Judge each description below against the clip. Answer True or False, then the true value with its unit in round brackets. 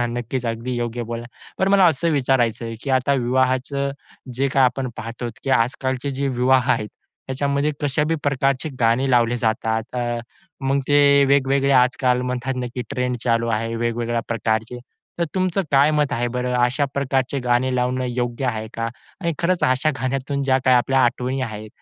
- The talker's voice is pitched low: True (130 Hz)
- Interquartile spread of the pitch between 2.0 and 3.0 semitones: True (2.5 semitones)